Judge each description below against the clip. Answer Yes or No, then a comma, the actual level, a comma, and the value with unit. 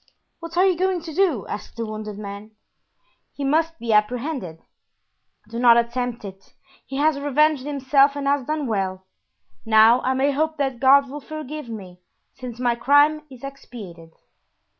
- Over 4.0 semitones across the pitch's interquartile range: Yes, average, 5.0 semitones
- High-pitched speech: Yes, very high, 260 Hz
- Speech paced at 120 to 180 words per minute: Yes, average, 160 wpm